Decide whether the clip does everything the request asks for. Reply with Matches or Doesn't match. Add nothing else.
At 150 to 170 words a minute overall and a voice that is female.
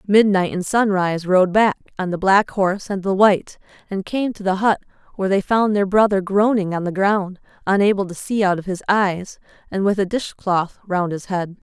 Doesn't match